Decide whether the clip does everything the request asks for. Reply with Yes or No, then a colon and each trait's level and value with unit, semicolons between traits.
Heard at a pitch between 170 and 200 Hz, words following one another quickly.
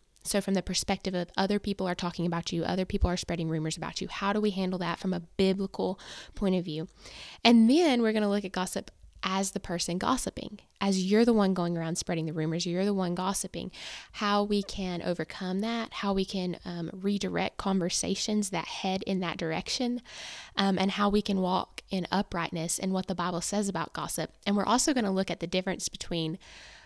Yes: high, 190 Hz; fast, 210 wpm